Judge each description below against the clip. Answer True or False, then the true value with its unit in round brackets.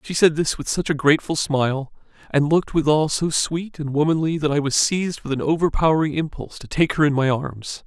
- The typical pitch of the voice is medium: True (150 Hz)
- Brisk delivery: True (220 wpm)